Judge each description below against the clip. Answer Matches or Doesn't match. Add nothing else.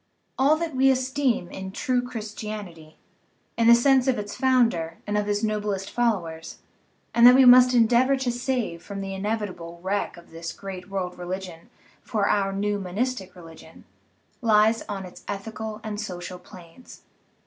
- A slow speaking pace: Doesn't match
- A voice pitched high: Matches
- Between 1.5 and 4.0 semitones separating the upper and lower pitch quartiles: Doesn't match